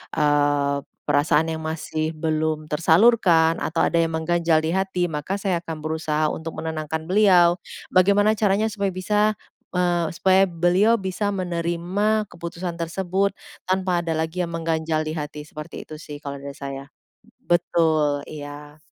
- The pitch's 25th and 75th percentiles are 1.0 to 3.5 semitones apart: Yes, average, 3.0 semitones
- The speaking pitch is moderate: Yes, medium, 165 Hz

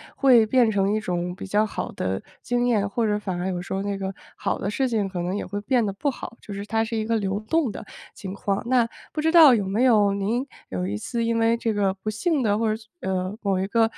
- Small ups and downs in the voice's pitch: No, average, 3.1 semitones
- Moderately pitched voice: No, high, 210 Hz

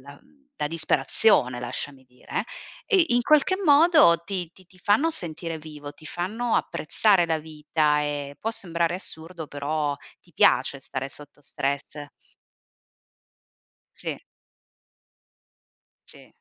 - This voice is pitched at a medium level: Yes, medium, 160 Hz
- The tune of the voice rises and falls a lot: Yes, wide, 6.0 semitones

